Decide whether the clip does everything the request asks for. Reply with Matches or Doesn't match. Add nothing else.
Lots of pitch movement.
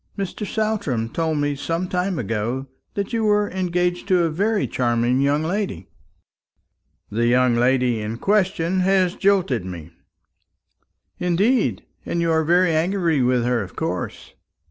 Matches